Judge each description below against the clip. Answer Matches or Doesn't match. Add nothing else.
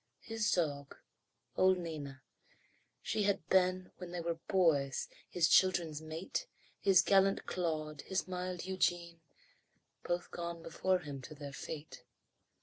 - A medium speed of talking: Doesn't match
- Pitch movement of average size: Matches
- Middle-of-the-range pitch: Matches